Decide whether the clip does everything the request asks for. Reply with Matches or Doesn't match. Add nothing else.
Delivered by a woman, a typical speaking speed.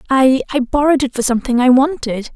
Matches